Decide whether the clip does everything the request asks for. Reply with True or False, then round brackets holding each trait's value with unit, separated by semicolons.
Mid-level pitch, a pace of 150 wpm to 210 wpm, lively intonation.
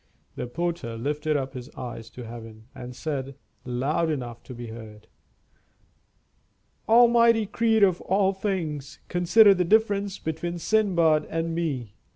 False (160 Hz; 135 wpm; 7.6 semitones)